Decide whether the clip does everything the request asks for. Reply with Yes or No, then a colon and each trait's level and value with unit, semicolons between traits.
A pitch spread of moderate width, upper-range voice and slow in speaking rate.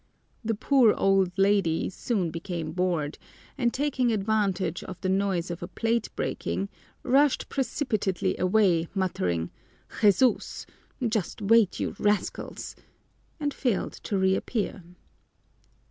Yes: average, 4.0 semitones; high, 200 Hz; slow, 115 wpm